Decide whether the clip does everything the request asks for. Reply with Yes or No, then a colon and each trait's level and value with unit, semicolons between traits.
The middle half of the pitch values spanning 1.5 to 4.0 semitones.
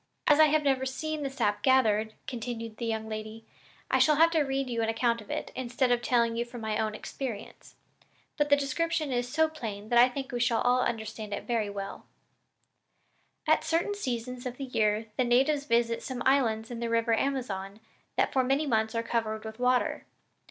Yes: average, 3.4 semitones